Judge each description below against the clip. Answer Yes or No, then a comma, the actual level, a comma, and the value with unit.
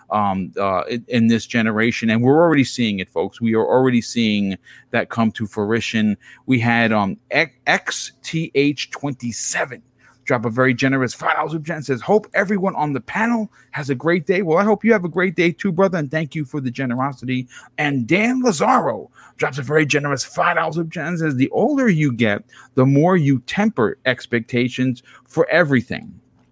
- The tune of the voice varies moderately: No, wide, 5.9 semitones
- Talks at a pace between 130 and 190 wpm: Yes, average, 185 wpm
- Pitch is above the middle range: No, low, 135 Hz